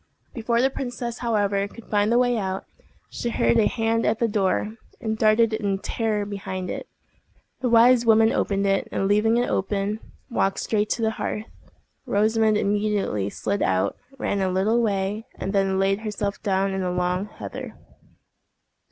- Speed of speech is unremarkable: Yes, average, 170 wpm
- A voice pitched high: Yes, high, 210 Hz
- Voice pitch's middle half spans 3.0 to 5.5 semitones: No, narrow, 2.5 semitones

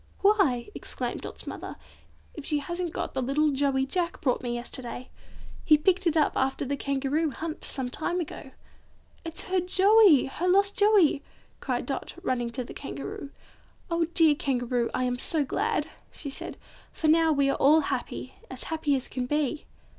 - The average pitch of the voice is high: Yes, very high, 295 Hz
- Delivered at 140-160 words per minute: No, average, 175 wpm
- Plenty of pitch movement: No, average, 4.2 semitones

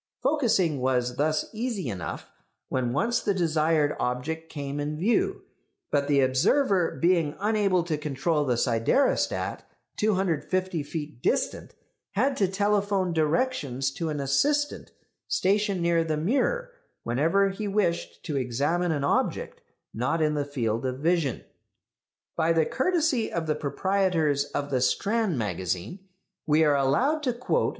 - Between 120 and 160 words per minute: Yes, average, 140 wpm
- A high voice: No, medium, 160 Hz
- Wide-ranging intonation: Yes, wide, 6.0 semitones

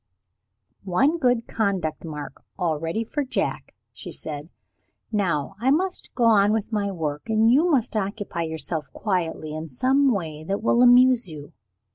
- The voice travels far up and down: Yes, wide, 7.0 semitones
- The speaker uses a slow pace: No, average, 150 wpm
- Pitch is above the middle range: Yes, high, 200 Hz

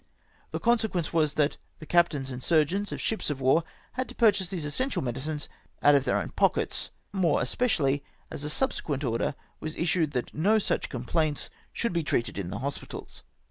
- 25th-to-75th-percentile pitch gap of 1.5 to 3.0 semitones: No, average, 5.1 semitones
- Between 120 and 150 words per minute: No, average, 185 wpm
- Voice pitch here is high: No, medium, 155 Hz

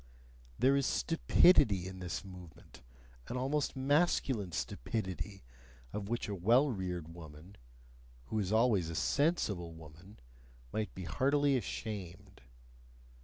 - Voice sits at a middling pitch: No, low, 100 Hz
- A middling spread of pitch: No, wide, 6.3 semitones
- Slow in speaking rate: Yes, slow, 120 wpm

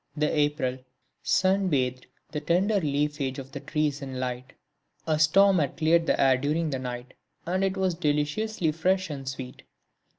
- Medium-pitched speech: Yes, medium, 150 Hz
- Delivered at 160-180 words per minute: Yes, average, 165 wpm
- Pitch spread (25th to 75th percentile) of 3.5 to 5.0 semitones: Yes, average, 4.5 semitones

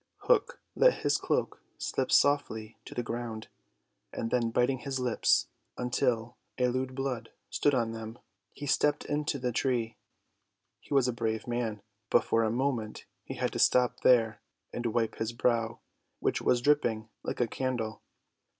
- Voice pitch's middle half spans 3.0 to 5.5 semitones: No, narrow, 2.5 semitones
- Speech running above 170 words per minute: No, average, 160 wpm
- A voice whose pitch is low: Yes, low, 120 Hz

